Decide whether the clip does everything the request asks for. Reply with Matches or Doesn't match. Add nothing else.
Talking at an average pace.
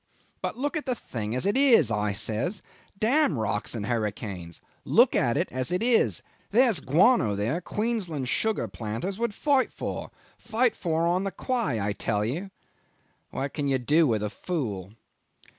Matches